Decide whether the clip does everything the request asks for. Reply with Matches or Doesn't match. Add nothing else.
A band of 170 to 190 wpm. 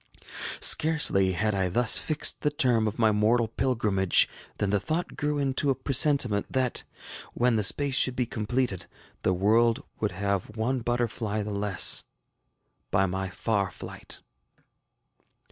Doesn't match